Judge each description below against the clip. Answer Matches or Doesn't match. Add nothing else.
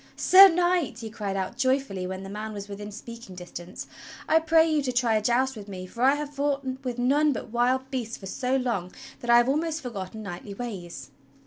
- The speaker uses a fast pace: Matches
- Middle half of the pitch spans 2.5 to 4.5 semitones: Doesn't match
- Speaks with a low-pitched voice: Doesn't match